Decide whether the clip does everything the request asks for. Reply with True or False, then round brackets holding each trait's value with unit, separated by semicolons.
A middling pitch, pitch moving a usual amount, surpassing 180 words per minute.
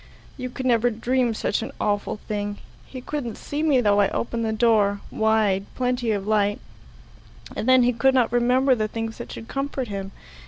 False (230 Hz; 3.1 semitones; 190 wpm)